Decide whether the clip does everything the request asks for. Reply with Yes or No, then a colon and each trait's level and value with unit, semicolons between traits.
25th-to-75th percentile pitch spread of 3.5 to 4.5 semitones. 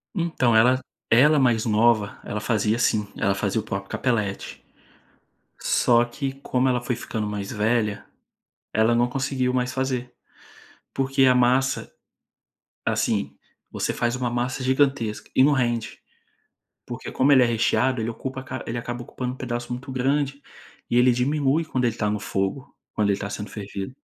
No: average, 3.0 semitones